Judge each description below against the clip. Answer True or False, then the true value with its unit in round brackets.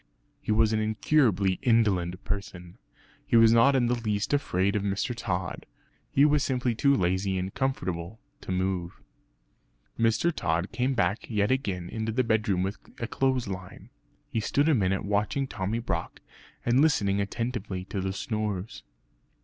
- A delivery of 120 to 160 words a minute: True (155 wpm)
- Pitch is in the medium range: False (105 Hz)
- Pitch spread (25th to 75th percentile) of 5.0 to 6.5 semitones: False (4.3 semitones)